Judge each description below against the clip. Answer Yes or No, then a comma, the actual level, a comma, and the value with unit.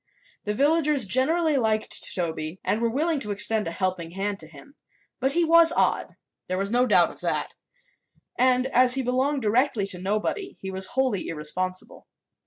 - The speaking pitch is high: Yes, high, 225 Hz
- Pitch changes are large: Yes, wide, 6.2 semitones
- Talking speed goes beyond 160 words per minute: Yes, average, 175 wpm